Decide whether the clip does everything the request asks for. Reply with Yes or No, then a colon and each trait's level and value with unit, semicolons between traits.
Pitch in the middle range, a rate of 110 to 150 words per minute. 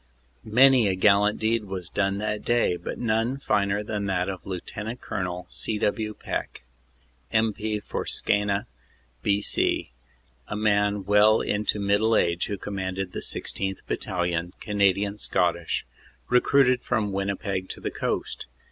No: low, 100 Hz; slow, 135 wpm